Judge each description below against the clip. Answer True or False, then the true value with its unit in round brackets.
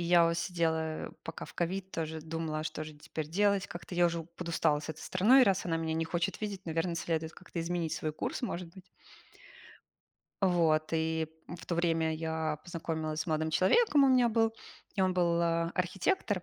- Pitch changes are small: True (2.3 semitones)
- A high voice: False (170 Hz)